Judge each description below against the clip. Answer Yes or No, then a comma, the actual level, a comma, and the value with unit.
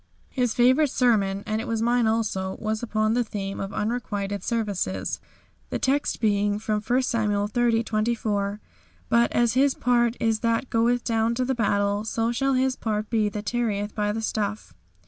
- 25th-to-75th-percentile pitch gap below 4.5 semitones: Yes, narrow, 2.5 semitones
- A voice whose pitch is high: Yes, high, 225 Hz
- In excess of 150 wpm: Yes, average, 175 wpm